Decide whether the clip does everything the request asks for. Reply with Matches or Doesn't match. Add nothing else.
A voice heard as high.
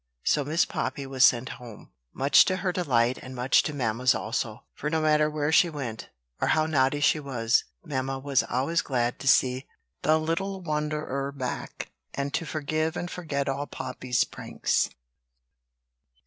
Doesn't match